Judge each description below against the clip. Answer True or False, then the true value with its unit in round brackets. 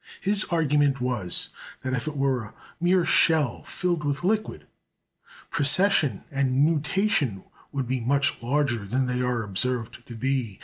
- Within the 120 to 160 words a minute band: True (145 wpm)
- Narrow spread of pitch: False (3.8 semitones)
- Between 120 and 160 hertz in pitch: True (135 Hz)